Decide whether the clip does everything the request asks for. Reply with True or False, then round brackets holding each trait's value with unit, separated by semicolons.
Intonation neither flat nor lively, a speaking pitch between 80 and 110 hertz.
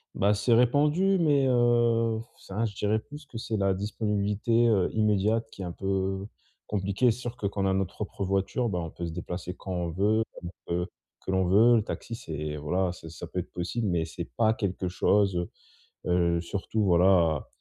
True (4.0 semitones; 100 Hz)